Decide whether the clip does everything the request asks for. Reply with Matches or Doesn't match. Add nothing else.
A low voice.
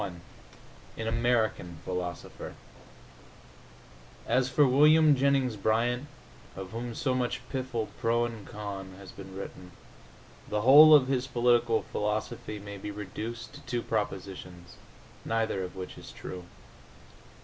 Matches